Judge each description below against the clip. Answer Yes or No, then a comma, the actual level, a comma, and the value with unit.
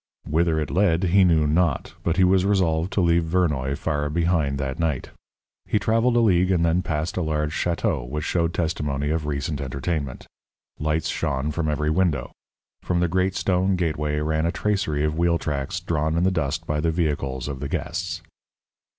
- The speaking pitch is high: No, very low, 80 Hz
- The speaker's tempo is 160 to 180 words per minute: No, average, 190 wpm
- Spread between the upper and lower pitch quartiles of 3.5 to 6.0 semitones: No, average, 2.9 semitones